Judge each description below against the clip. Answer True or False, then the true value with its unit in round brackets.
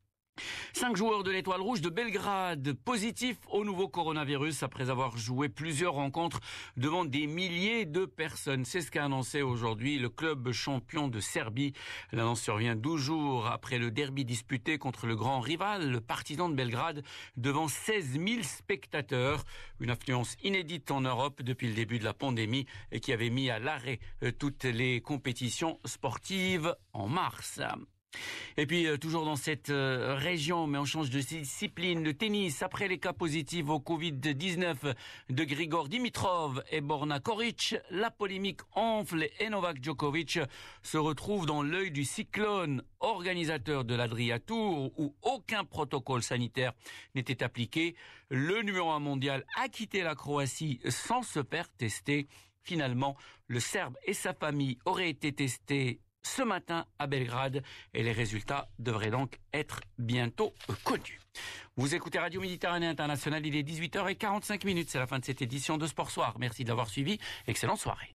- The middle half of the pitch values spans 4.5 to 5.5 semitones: True (5.1 semitones)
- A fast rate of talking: True (160 wpm)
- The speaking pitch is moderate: True (145 Hz)